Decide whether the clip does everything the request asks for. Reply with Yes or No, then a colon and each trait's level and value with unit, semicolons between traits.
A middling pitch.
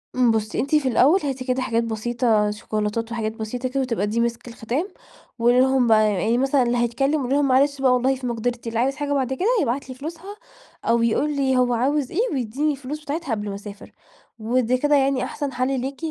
No: very high, 255 Hz